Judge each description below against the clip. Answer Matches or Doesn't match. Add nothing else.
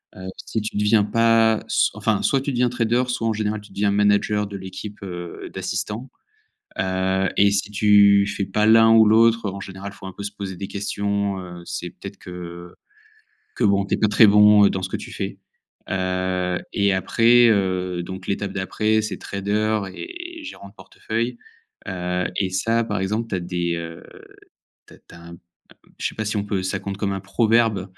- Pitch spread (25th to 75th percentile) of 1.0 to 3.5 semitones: Matches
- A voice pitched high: Doesn't match